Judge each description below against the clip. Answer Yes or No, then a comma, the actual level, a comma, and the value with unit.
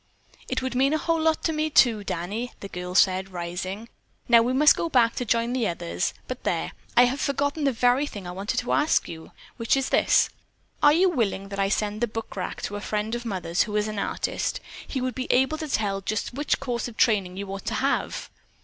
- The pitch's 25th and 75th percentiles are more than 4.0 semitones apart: Yes, average, 5.0 semitones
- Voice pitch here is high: Yes, high, 230 Hz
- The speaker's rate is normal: No, fast, 230 wpm